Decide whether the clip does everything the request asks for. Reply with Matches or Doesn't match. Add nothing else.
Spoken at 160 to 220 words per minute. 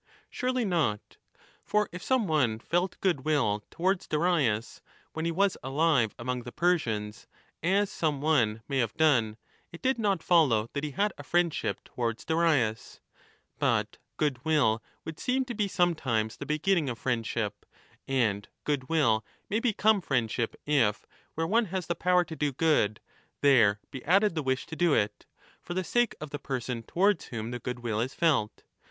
Matches